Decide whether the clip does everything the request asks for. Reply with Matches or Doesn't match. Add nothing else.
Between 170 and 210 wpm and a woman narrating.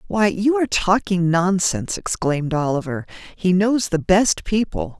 Doesn't match